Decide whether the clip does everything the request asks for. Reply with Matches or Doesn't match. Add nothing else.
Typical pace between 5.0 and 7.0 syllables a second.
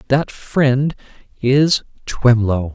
Doesn't match